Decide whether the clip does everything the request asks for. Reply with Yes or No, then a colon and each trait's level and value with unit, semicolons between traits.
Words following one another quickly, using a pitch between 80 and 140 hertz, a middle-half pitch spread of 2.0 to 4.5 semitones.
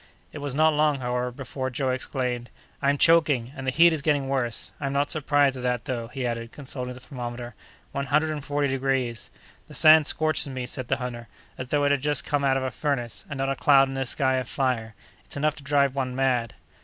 Yes: fast, 230 wpm; low, 135 Hz; narrow, 2.5 semitones